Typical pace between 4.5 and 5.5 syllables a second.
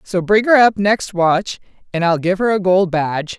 Yes: 4.7 syllables/s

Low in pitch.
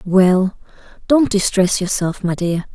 No: high, 190 Hz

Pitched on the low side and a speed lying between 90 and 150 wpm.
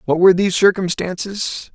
No: medium, 185 Hz; average, 140 wpm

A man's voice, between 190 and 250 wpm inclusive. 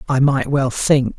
Yes: male; average, 200 wpm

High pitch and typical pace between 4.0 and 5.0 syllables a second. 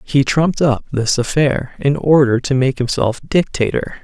No: low, 135 Hz; 4.5 syllables/s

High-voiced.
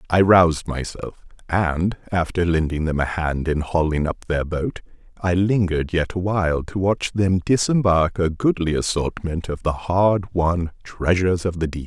No: very low, 85 Hz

